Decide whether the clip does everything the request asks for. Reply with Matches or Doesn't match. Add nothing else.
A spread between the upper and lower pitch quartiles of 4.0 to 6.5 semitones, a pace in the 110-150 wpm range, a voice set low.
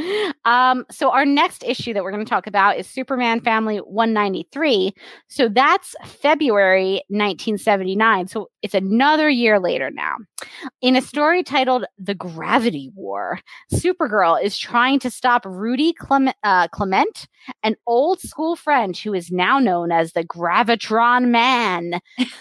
Doesn't match